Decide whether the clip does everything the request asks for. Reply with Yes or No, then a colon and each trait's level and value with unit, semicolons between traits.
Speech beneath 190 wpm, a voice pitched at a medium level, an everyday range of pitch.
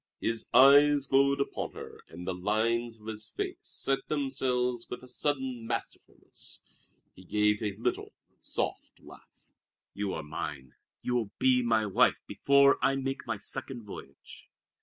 No: average, 150 wpm; low, 120 Hz; average, 4.3 semitones